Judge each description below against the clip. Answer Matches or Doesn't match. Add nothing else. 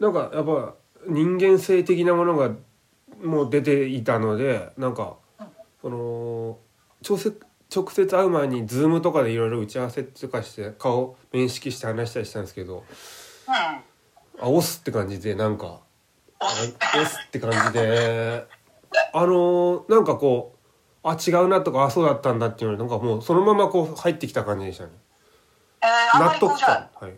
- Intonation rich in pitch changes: Matches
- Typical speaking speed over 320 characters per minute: Doesn't match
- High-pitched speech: Doesn't match